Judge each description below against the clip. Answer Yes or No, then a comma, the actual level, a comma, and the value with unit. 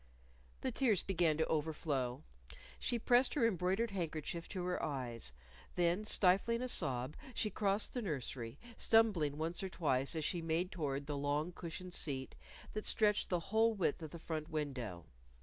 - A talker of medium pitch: Yes, medium, 170 Hz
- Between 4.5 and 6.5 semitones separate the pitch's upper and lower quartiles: Yes, average, 5.3 semitones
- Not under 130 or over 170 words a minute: Yes, average, 165 wpm